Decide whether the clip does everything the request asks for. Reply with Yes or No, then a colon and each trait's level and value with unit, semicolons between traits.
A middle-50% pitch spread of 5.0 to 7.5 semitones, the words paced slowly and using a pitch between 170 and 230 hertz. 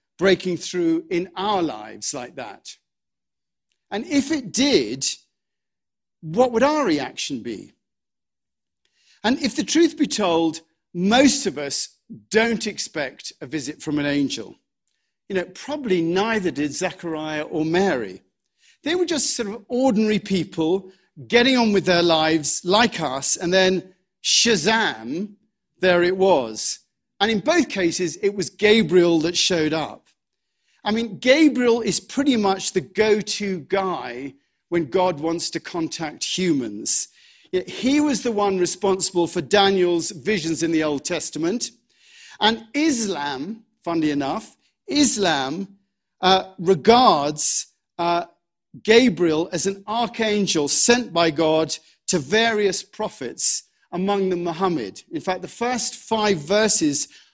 Yes: average, 5.3 semitones; slow, 130 wpm; high, 190 Hz